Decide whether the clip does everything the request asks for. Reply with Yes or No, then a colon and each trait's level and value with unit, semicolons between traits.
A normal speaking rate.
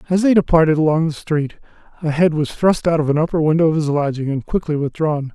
No: fast, 235 wpm